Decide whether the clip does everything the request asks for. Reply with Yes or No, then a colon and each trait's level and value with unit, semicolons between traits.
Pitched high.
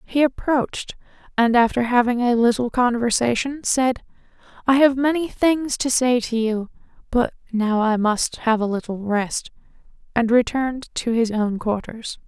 Yes: high, 240 Hz